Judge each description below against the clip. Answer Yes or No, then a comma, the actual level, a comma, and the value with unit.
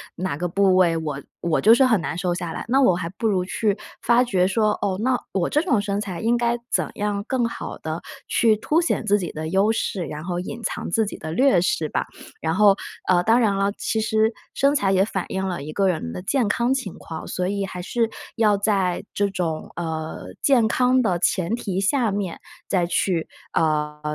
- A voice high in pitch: Yes, high, 195 Hz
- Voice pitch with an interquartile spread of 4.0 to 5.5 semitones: Yes, average, 4.4 semitones